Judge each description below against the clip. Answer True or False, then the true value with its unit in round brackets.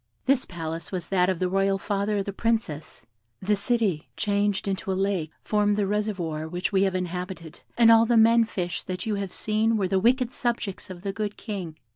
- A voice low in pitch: False (195 Hz)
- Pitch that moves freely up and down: False (2.8 semitones)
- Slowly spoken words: False (205 wpm)